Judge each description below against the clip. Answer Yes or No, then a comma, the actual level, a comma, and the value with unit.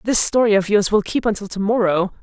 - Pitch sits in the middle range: No, high, 205 Hz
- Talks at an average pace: No, fast, 245 wpm